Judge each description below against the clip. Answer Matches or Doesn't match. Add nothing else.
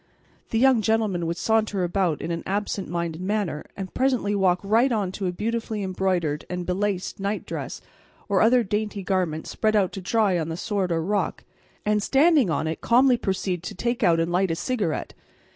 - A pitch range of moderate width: Matches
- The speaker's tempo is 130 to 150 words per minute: Doesn't match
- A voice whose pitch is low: Doesn't match